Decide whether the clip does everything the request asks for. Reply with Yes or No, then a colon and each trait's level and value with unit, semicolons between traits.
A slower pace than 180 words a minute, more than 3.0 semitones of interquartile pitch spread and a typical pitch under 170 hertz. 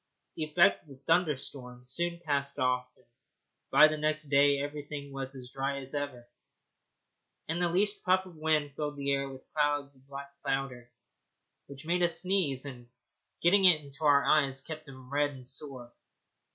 No: average, 170 wpm; narrow, 2.4 semitones; medium, 140 Hz